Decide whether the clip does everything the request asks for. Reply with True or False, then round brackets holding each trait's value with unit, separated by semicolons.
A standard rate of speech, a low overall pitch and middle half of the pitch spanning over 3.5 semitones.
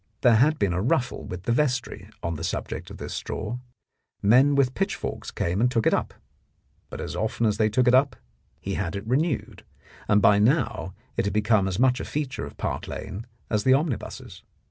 False (210 wpm; 115 Hz; 4.3 semitones)